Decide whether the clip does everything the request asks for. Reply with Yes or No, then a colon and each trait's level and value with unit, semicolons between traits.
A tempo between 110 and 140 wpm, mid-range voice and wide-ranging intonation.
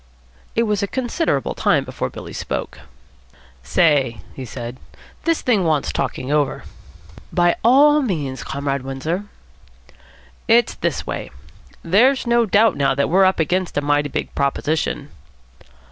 Yes: slow, 135 wpm; medium, 165 Hz; wide, 7.6 semitones